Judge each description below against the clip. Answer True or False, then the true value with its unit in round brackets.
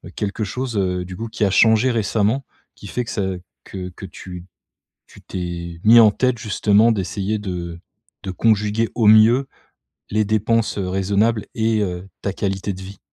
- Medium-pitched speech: False (105 Hz)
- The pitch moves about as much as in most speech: True (3.0 semitones)